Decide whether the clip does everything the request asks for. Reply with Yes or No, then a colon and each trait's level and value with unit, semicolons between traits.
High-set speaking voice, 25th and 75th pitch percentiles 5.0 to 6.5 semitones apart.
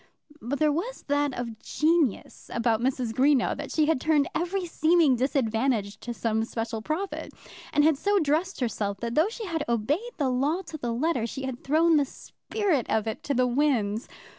Yes: very high, 275 Hz; wide, 5.4 semitones